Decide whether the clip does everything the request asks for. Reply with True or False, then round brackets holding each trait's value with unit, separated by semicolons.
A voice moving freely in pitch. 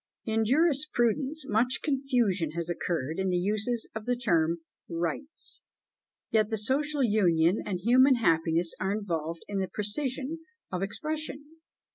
True (7.0 semitones)